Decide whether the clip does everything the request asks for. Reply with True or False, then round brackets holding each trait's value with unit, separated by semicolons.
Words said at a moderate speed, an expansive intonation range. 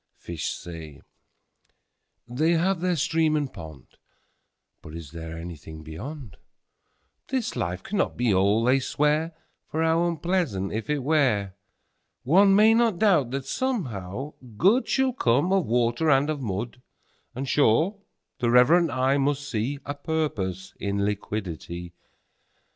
False (115 wpm; 8.5 semitones)